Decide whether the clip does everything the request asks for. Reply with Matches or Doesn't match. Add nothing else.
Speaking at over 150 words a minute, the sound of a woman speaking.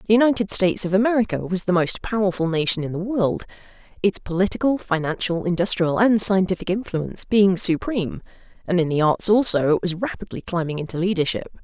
Matches